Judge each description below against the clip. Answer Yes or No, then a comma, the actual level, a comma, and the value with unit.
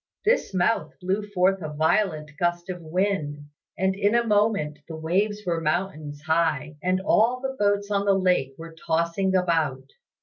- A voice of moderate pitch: Yes, medium, 180 Hz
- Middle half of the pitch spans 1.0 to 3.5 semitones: No, average, 4.2 semitones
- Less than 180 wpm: Yes, average, 165 wpm